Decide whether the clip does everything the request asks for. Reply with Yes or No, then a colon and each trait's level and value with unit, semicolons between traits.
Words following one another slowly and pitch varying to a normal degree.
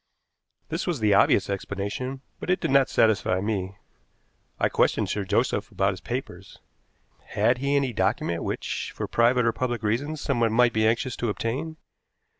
No: average, 165 wpm; average, 4.3 semitones